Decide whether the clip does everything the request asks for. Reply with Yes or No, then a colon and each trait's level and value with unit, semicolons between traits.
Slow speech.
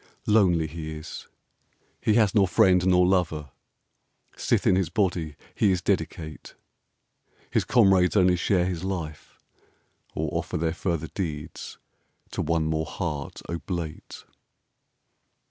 Yes: slow, 125 wpm